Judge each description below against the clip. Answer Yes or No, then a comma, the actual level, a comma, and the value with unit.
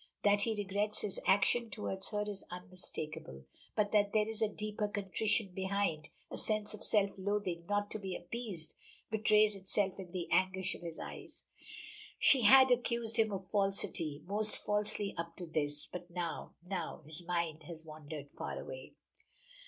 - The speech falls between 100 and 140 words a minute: No, average, 165 wpm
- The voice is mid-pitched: No, high, 195 Hz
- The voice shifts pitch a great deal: No, average, 3.3 semitones